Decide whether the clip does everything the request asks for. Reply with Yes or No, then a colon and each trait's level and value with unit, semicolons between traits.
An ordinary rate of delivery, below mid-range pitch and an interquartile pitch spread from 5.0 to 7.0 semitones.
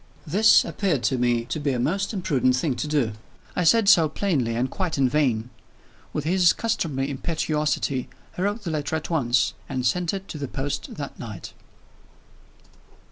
No: average, 175 wpm; medium, 150 Hz; wide, 5.6 semitones